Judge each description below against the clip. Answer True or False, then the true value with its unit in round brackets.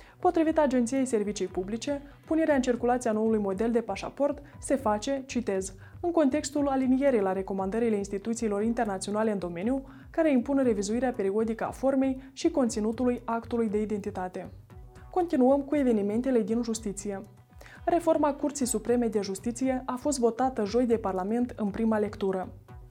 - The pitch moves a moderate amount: True (4.3 semitones)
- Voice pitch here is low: False (235 Hz)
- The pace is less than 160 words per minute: True (140 wpm)